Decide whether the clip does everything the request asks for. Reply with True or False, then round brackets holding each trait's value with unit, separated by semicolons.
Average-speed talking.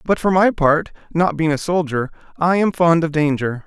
False (215 wpm)